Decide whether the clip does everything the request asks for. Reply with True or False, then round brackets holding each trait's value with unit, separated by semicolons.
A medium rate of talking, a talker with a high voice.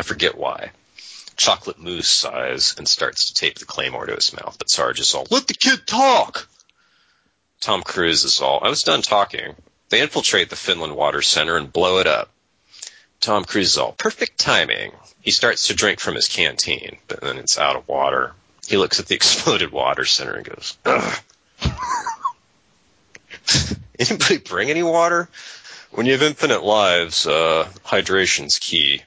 True (170 wpm; 270 Hz)